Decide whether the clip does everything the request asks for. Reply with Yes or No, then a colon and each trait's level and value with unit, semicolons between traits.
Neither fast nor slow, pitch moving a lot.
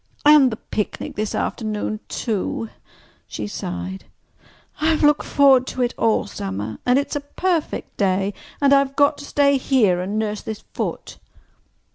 Yes: average, 145 wpm; wide, 6.2 semitones